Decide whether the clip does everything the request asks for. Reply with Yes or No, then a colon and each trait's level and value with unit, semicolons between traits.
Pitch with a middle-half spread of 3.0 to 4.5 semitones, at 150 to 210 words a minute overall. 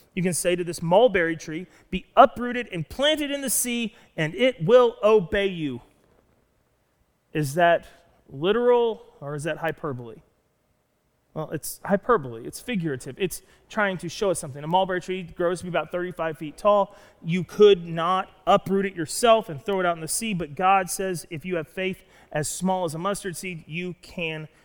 Yes: average, 3.8 semitones; average, 185 wpm